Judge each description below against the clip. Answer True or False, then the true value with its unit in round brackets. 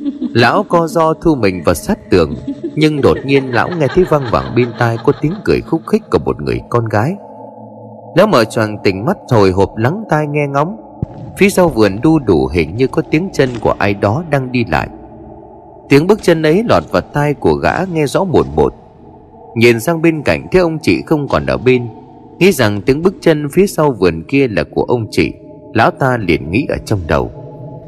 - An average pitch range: False (6.8 semitones)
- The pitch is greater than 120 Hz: True (140 Hz)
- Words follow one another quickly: False (215 wpm)